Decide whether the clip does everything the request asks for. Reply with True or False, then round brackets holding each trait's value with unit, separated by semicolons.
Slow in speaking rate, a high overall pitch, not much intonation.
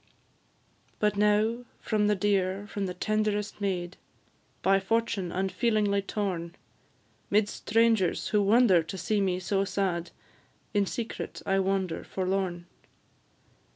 True (120 wpm; 200 Hz; 2.1 semitones)